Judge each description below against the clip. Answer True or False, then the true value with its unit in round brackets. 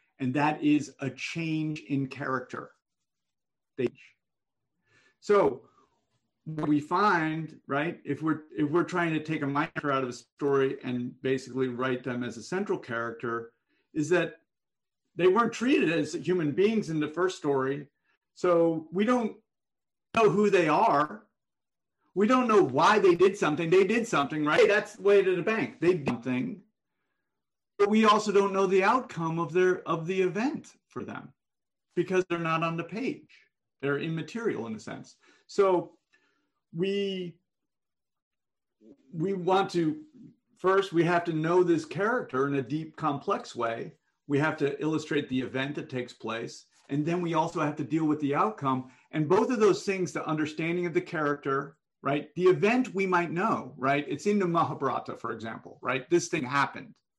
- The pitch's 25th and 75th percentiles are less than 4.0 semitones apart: False (5.1 semitones)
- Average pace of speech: True (170 wpm)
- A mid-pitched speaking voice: True (165 Hz)